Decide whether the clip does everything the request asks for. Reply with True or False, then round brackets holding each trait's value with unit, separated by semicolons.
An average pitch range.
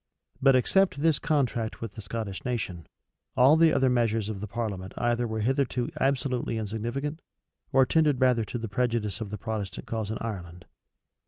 True (3.7 semitones)